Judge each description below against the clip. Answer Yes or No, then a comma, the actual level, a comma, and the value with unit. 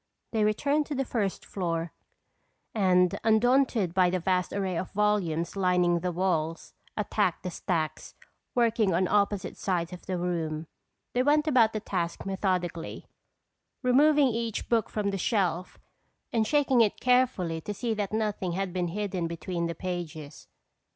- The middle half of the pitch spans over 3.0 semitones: Yes, average, 4.1 semitones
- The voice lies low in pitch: No, high, 190 Hz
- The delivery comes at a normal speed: Yes, average, 150 wpm